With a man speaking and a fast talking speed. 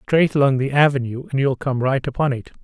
Yes: male; fast, 230 wpm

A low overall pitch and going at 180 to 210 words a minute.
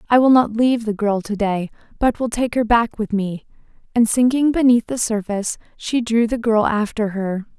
No: high, 225 Hz; fast, 205 wpm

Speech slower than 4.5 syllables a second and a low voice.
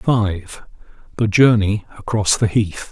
Yes: 4.1 syllables/s; low, 105 Hz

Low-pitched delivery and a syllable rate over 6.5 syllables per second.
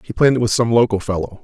Yes: low, 110 Hz; 7.5 syllables/s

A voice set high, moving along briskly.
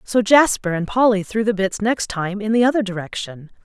Yes: high, 210 Hz; fast, 215 wpm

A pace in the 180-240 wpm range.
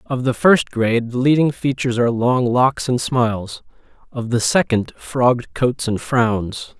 No: average, 170 wpm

